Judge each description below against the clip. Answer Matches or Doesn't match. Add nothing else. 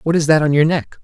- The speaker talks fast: Matches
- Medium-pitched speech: Matches